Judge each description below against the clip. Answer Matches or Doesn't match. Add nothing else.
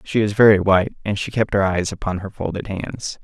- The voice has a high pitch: Doesn't match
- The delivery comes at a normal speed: Doesn't match